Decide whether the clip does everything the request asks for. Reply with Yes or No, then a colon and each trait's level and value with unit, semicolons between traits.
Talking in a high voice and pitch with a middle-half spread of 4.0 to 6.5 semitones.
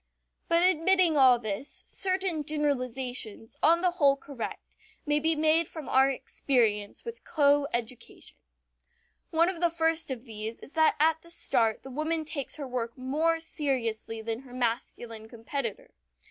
Yes: very high, 280 Hz; average, 5.1 semitones